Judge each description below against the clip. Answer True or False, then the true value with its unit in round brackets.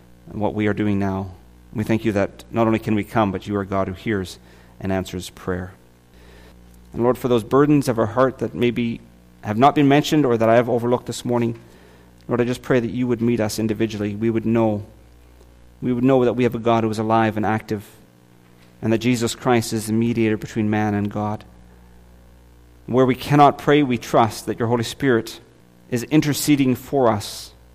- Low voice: True (110 Hz)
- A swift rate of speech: True (210 wpm)